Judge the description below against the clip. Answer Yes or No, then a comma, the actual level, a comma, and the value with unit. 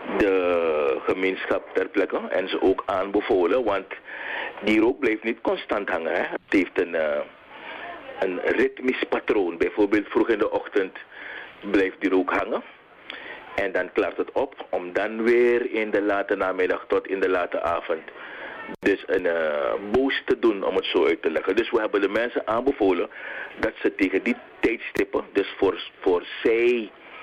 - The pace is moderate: Yes, average, 170 wpm